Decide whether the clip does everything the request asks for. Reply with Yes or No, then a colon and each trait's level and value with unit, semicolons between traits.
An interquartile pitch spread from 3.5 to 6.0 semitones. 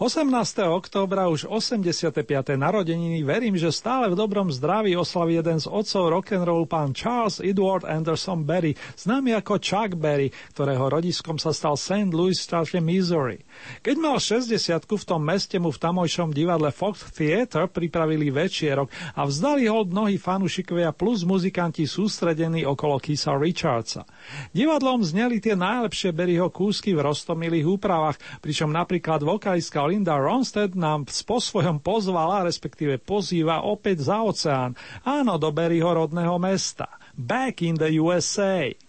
Yes: average, 4.3 semitones